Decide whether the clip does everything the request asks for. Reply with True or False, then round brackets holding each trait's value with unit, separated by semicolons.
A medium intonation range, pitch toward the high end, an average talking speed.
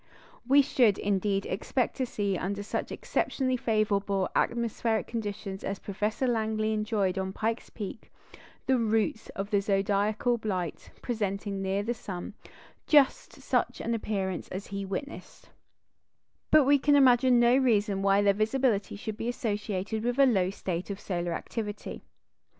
True (3.2 semitones; 210 Hz; 145 wpm)